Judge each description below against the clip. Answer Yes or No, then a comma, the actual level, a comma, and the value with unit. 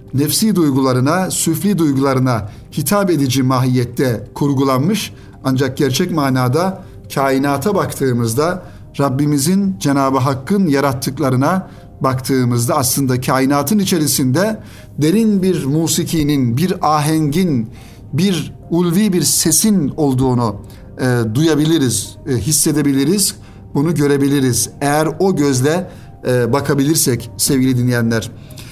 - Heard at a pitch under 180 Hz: Yes, medium, 140 Hz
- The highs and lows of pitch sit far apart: No, average, 3.8 semitones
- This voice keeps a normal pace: No, slow, 90 wpm